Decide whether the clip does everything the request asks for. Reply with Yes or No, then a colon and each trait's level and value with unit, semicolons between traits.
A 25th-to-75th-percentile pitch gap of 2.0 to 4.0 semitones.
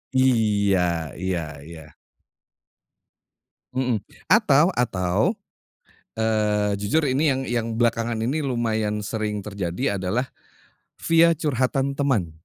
No: average, 4.6 semitones